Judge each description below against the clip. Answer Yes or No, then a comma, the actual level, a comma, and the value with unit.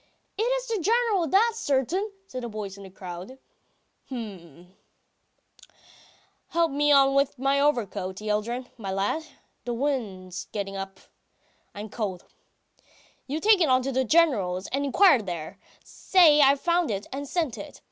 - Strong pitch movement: Yes, wide, 7.9 semitones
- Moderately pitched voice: No, very high, 260 Hz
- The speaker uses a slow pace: No, average, 150 wpm